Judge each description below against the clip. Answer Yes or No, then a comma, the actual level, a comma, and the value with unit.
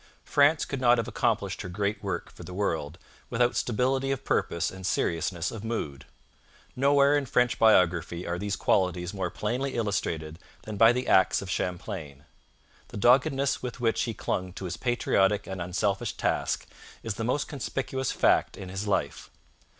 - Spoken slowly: No, average, 165 wpm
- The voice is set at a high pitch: No, low, 105 Hz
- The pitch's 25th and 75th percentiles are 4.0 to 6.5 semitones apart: Yes, average, 5.3 semitones